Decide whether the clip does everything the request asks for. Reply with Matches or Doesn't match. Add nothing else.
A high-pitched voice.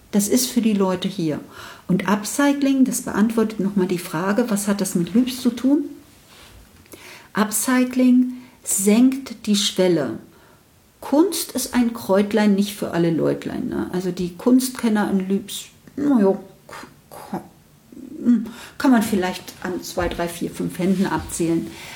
Matches